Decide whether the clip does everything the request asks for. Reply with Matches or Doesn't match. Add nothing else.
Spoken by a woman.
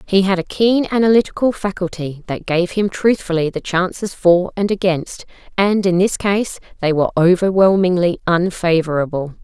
Matches